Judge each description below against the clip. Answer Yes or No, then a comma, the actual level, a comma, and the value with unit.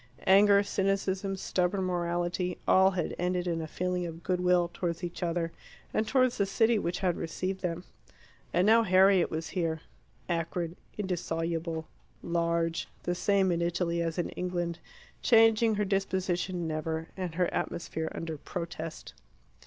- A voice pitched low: No, medium, 180 Hz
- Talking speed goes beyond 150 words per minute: No, average, 145 wpm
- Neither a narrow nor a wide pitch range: No, narrow, 2.2 semitones